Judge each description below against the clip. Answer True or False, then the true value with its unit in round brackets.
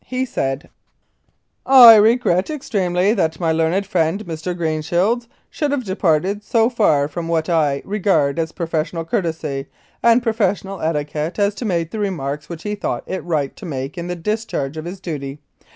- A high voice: False (175 Hz)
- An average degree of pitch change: True (4.8 semitones)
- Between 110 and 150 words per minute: False (170 wpm)